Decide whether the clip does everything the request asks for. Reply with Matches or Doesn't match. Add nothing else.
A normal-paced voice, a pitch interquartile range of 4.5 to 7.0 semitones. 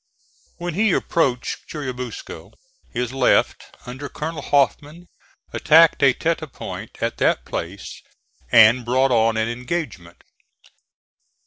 Doesn't match